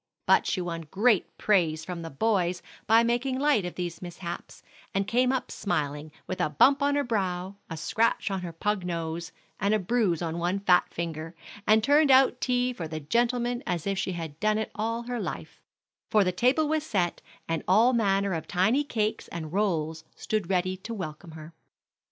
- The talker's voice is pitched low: No, high, 195 Hz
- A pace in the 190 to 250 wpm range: Yes, average, 195 wpm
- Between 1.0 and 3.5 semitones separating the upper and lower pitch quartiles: No, wide, 5.5 semitones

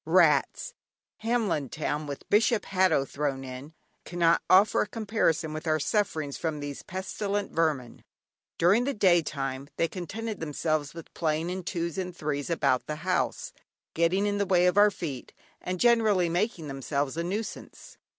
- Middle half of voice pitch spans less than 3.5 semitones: No, average, 4.7 semitones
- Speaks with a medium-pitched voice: Yes, medium, 170 Hz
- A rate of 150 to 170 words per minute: Yes, average, 160 wpm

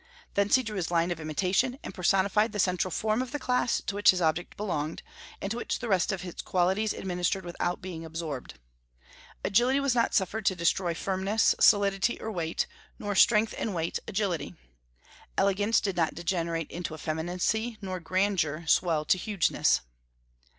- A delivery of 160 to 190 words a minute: Yes, average, 170 wpm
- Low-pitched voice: No, high, 190 Hz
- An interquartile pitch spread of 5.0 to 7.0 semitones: No, average, 3.7 semitones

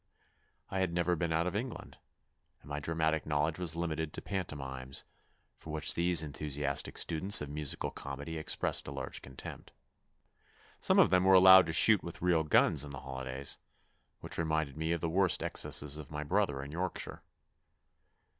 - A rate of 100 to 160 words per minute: No, average, 170 wpm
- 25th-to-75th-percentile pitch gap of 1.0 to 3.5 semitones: Yes, average, 3.1 semitones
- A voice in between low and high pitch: No, very low, 80 Hz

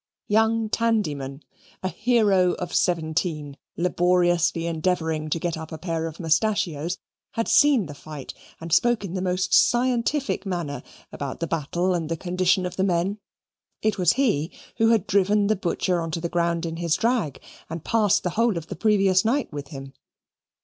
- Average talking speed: Yes, average, 175 wpm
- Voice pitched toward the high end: No, medium, 180 Hz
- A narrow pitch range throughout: No, average, 4.4 semitones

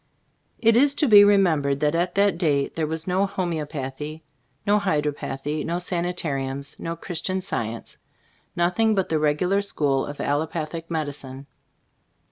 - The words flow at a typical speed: No, slow, 130 wpm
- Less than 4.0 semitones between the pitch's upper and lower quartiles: No, average, 4.3 semitones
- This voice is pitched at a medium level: Yes, medium, 160 Hz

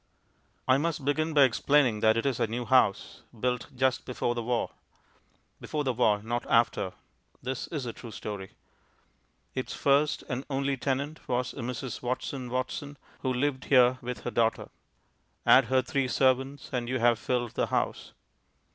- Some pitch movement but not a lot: No, narrow, 2.3 semitones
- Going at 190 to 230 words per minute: No, average, 165 wpm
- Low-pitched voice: Yes, low, 125 Hz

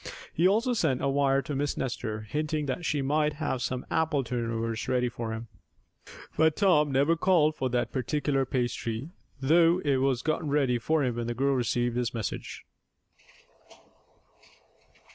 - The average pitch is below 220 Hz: Yes, low, 135 Hz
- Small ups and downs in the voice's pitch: No, average, 3.9 semitones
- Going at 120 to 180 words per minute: Yes, average, 160 wpm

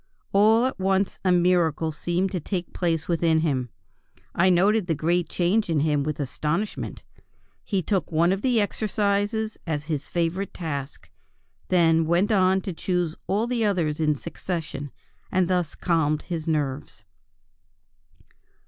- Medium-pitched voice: Yes, medium, 175 Hz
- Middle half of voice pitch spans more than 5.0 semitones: No, average, 3.5 semitones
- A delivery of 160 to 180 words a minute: No, average, 145 wpm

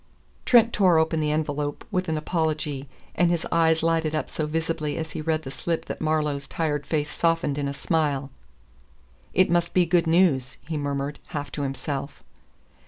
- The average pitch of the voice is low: No, medium, 155 Hz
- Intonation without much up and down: Yes, narrow, 2.2 semitones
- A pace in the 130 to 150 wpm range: No, average, 175 wpm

